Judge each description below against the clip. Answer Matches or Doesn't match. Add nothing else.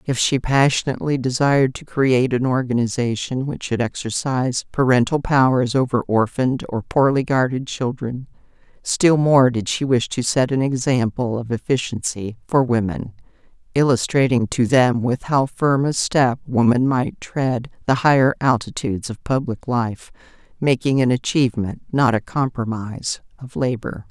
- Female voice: Matches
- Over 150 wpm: Doesn't match